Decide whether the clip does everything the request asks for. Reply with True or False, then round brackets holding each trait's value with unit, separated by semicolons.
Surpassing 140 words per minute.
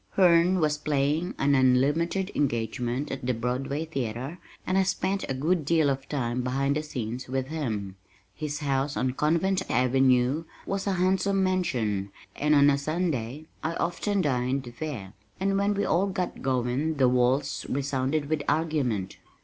True (155 wpm)